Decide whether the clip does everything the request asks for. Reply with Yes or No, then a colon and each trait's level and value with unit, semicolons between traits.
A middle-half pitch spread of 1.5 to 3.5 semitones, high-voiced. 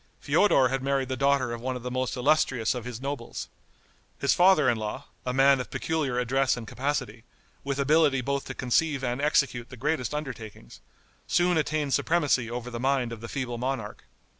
No: narrow, 2.5 semitones; low, 130 Hz